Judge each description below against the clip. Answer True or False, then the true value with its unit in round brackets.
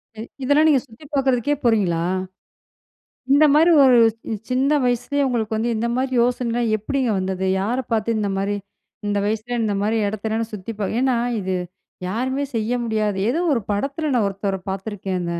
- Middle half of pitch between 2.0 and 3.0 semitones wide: False (3.9 semitones)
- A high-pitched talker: True (225 Hz)